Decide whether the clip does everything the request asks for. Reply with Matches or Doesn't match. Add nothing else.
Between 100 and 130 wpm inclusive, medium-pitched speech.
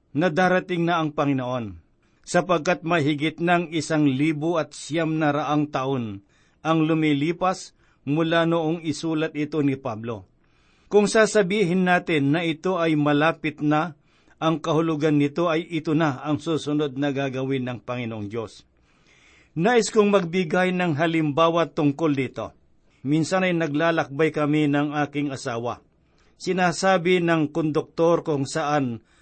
Matches